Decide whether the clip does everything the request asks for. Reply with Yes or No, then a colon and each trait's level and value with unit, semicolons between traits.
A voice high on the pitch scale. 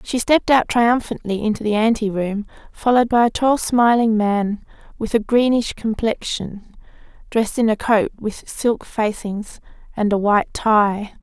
Yes: high, 220 Hz